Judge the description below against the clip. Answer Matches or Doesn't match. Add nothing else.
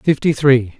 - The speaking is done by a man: Matches